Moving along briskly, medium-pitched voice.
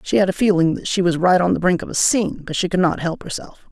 Yes: fast, 325 wpm; medium, 175 Hz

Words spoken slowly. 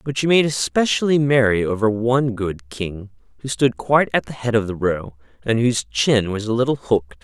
No: fast, 205 wpm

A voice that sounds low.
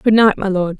No: high, 200 Hz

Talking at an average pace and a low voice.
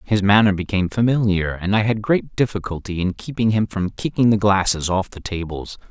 Yes: average, 195 wpm; low, 100 Hz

